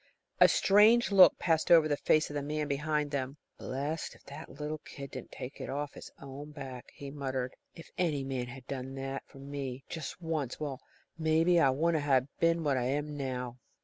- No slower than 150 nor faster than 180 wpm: No, fast, 205 wpm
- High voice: No, medium, 145 Hz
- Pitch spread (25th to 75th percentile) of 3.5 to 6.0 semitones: No, narrow, 2.6 semitones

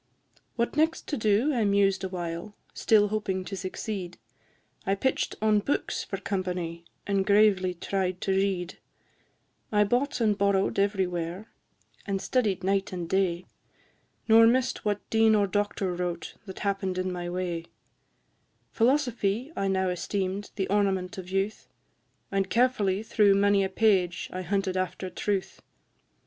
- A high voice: Yes, high, 195 Hz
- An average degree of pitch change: No, narrow, 2.2 semitones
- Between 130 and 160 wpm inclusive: Yes, average, 145 wpm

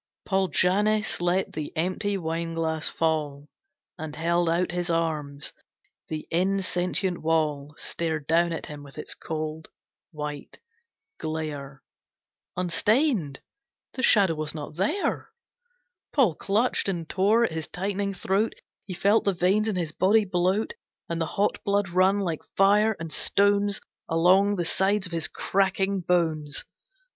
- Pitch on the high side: No, medium, 175 Hz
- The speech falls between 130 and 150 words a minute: Yes, average, 140 wpm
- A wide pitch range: No, average, 3.7 semitones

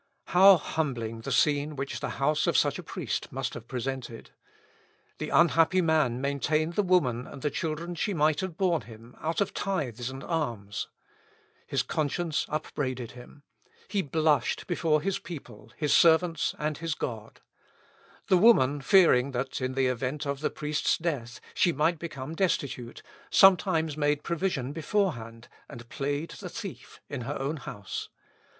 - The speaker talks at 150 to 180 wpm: Yes, average, 155 wpm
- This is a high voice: No, medium, 150 Hz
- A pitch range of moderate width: Yes, average, 4.4 semitones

